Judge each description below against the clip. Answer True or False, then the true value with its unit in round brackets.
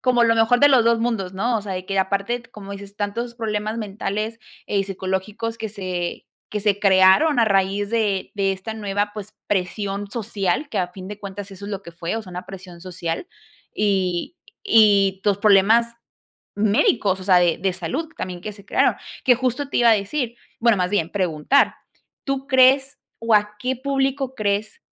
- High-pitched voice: True (205 Hz)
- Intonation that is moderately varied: True (3.3 semitones)